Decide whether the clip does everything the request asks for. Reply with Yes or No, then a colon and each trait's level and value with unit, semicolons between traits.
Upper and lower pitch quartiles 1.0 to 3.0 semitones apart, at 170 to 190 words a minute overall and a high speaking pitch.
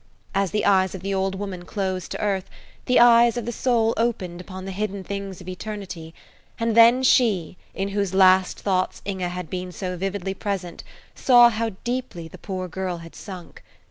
Yes: average, 2.7 semitones; average, 185 wpm; high, 195 Hz